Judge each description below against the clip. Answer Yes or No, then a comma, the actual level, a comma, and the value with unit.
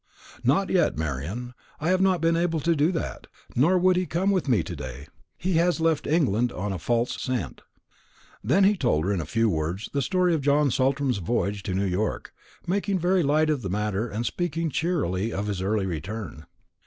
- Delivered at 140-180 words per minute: No, fast, 205 wpm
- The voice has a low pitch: Yes, low, 130 Hz